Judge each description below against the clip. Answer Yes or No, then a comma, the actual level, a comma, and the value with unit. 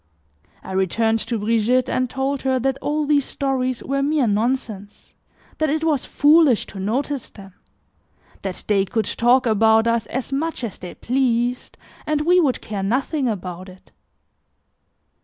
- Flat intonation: No, average, 4.3 semitones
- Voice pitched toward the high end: Yes, very high, 250 Hz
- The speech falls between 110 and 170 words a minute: Yes, average, 155 wpm